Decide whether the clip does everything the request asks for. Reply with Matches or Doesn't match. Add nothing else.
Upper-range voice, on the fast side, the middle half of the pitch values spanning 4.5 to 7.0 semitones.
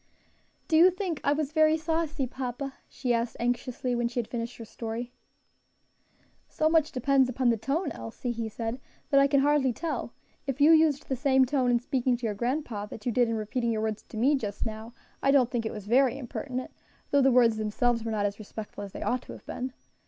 Doesn't match